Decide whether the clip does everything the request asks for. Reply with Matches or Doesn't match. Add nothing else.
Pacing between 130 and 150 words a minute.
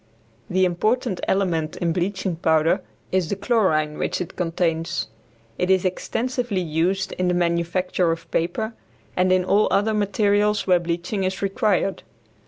Matches